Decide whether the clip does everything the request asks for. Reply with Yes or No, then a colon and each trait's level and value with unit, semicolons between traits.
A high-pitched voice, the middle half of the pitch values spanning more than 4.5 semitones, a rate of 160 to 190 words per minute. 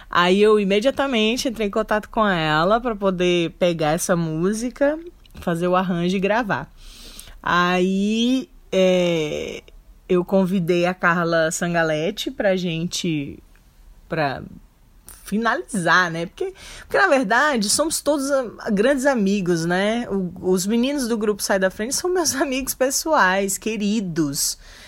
No: high, 195 Hz; average, 5.1 semitones; average, 125 wpm